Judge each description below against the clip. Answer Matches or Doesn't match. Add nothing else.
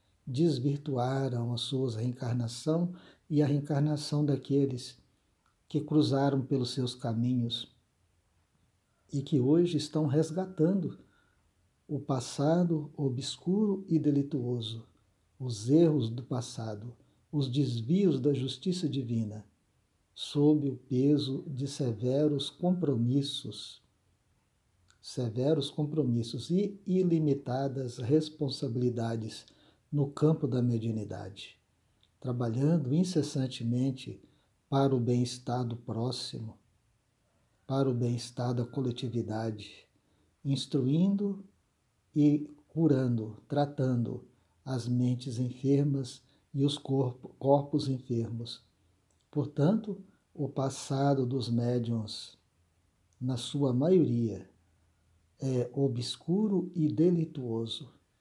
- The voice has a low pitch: Matches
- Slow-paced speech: Matches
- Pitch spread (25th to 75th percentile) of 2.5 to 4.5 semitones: Matches